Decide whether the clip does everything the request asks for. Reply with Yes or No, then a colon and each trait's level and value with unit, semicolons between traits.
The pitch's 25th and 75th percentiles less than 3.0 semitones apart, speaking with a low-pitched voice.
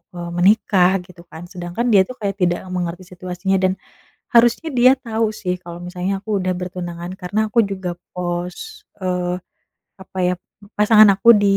No: narrow, 2.5 semitones; medium, 185 Hz